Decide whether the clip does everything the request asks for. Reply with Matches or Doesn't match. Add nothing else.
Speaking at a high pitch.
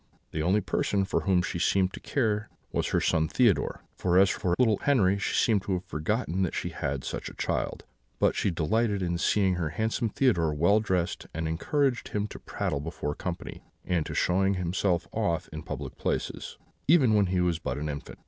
Doesn't match